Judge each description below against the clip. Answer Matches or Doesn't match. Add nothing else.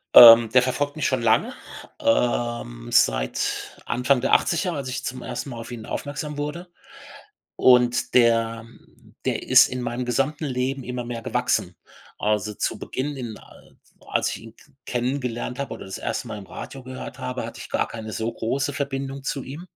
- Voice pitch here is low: Matches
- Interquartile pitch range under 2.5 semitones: Doesn't match